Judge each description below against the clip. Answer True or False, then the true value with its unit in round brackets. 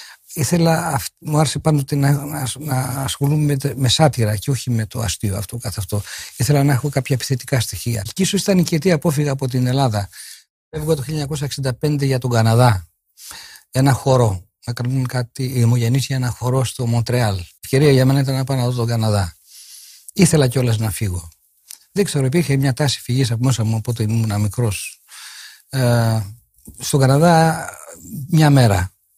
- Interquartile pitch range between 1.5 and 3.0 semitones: False (3.8 semitones)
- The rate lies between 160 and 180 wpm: True (170 wpm)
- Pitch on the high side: False (130 Hz)